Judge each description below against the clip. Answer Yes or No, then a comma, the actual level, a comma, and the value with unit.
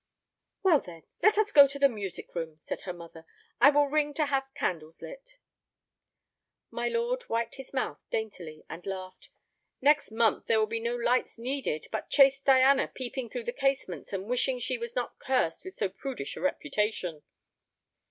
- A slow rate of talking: No, average, 175 wpm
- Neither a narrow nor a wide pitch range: No, wide, 6.2 semitones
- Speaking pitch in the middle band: No, very high, 250 Hz